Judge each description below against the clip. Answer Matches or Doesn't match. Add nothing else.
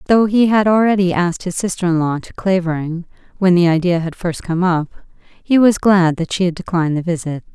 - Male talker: Doesn't match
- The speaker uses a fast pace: Matches